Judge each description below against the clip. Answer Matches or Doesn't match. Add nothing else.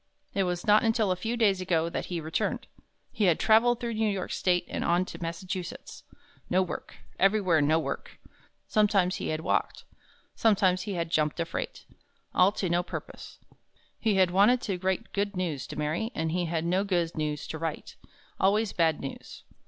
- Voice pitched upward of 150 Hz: Matches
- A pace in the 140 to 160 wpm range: Doesn't match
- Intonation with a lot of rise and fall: Doesn't match